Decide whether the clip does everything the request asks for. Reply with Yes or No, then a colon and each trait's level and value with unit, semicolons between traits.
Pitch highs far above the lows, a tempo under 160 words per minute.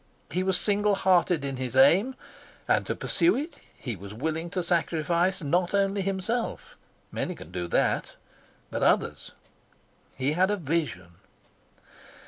Yes: wide, 5.9 semitones; average, 140 wpm